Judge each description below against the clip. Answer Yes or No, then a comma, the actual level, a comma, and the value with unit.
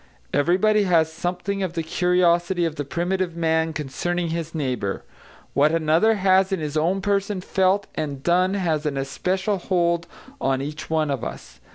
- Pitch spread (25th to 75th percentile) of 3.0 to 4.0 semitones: Yes, average, 3.3 semitones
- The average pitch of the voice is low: No, medium, 170 Hz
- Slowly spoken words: No, average, 165 wpm